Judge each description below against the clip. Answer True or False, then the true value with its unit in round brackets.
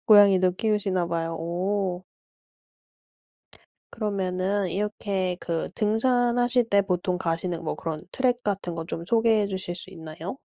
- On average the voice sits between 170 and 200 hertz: True (190 Hz)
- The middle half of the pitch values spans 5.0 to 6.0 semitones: False (3.2 semitones)